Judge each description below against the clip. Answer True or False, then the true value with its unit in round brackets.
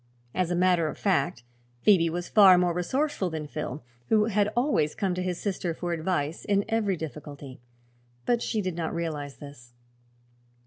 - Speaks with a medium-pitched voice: True (175 Hz)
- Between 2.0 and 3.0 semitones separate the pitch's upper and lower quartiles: False (4.3 semitones)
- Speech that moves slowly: False (170 wpm)